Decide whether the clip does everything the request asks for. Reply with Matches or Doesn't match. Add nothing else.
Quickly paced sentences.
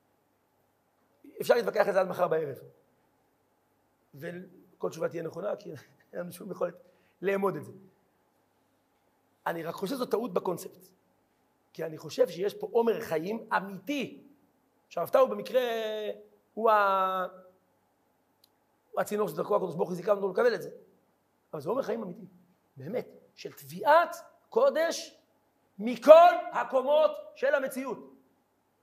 Doesn't match